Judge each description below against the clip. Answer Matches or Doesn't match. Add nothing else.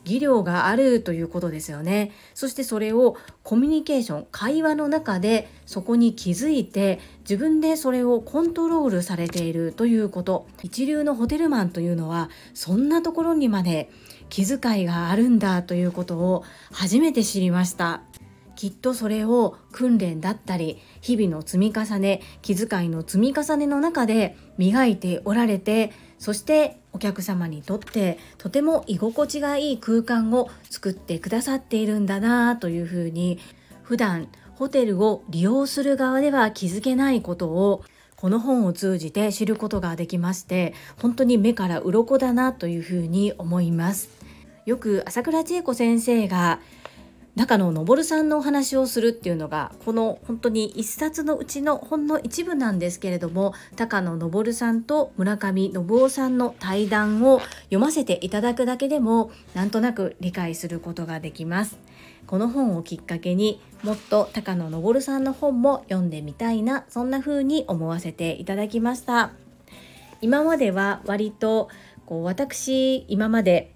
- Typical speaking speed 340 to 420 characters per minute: Doesn't match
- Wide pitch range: Matches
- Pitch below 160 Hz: Doesn't match